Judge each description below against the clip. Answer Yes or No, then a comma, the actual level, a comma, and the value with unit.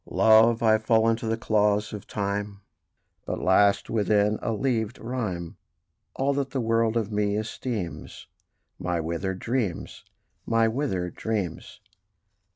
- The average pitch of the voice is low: Yes, low, 110 Hz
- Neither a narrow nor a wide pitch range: No, narrow, 2.1 semitones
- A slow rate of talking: Yes, slow, 130 wpm